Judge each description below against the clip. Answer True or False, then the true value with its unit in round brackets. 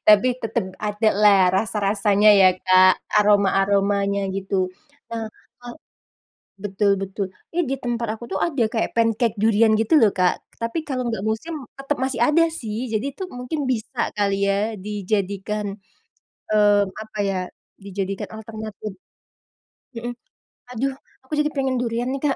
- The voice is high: True (215 Hz)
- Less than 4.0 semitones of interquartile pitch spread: True (3.3 semitones)